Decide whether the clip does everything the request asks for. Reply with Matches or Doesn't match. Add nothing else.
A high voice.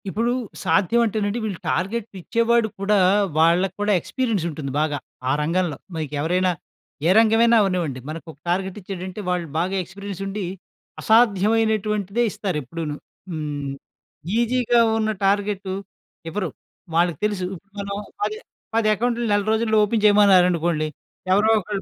Matches